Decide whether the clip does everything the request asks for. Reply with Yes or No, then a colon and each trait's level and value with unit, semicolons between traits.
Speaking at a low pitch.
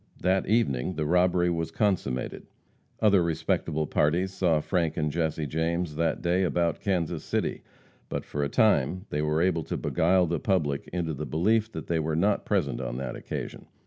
Yes: very low, 85 Hz